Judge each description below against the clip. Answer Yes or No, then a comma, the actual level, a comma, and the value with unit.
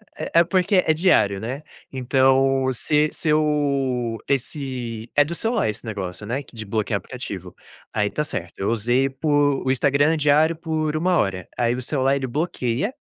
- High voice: No, low, 135 Hz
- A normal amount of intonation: Yes, average, 4.4 semitones